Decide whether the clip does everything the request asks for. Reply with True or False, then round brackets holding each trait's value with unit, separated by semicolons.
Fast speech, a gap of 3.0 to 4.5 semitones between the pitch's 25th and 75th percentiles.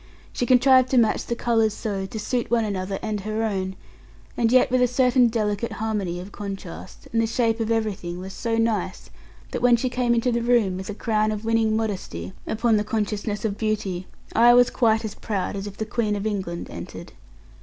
False (210 wpm; 2.6 semitones)